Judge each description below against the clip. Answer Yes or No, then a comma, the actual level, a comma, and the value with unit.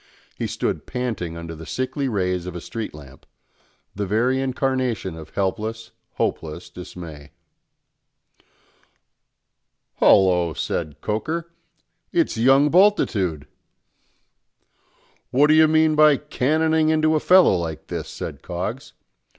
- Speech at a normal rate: No, slow, 115 wpm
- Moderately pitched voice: No, low, 115 Hz